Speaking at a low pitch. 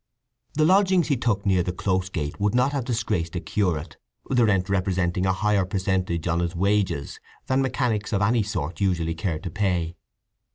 Yes: very low, 95 Hz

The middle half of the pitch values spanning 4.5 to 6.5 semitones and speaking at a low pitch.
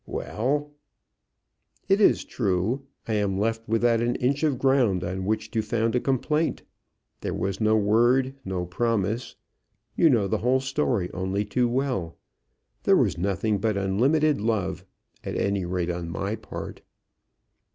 Yes: average, 4.8 semitones; low, 110 Hz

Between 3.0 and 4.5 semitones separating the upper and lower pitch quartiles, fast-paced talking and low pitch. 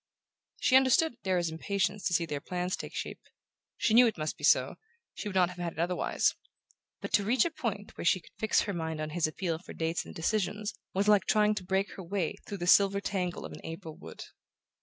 No: average, 3.5 semitones; fast, 225 wpm; high, 190 Hz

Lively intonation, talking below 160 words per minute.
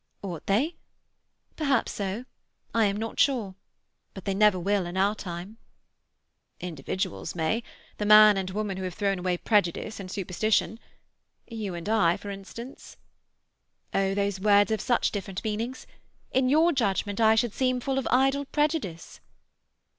No: average, 3.4 semitones; average, 150 wpm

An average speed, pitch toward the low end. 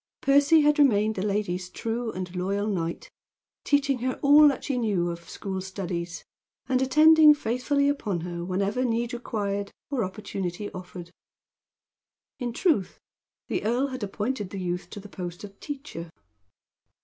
No: average, 150 wpm; high, 210 Hz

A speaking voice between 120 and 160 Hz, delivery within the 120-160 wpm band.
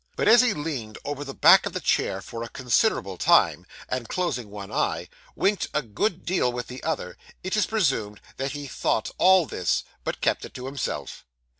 No: low, 135 Hz; average, 195 wpm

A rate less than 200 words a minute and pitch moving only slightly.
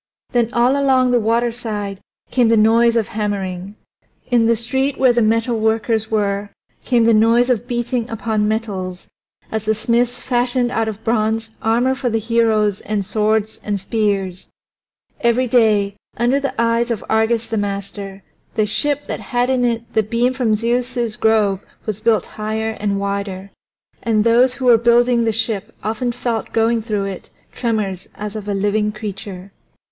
Yes: average, 165 wpm; narrow, 2.3 semitones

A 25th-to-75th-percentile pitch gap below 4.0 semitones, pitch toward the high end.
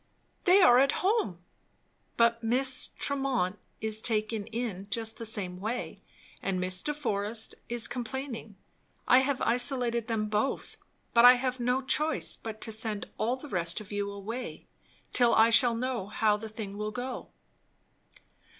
Yes: average, 3.1 semitones; high, 230 Hz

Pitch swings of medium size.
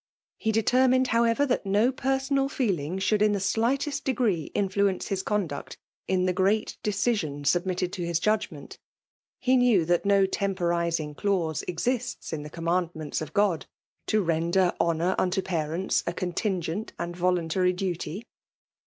Yes: average, 4.2 semitones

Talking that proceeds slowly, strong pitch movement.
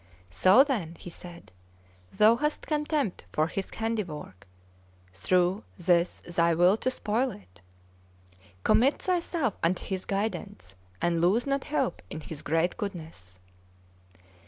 Yes: slow, 125 wpm; wide, 5.8 semitones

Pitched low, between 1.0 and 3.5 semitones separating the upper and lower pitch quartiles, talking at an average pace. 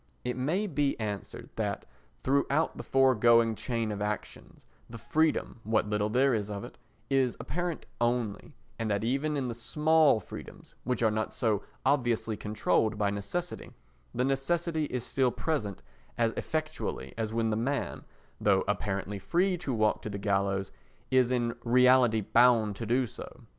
No: low, 120 Hz; average, 4.2 semitones; average, 160 wpm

